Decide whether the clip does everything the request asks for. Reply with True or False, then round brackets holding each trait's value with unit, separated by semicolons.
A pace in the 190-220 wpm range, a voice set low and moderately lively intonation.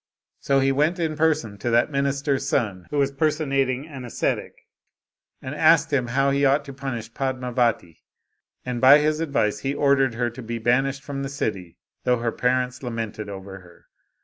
False (175 wpm; 130 Hz; 3.0 semitones)